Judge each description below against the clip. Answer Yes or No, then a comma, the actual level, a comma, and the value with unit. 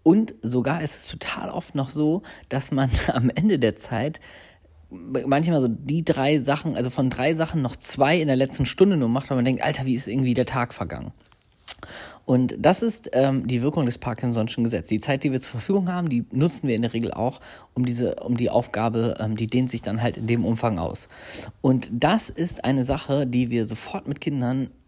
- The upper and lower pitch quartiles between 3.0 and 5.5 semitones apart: Yes, average, 3.7 semitones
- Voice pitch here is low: Yes, low, 130 Hz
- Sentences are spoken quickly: Yes, fast, 215 wpm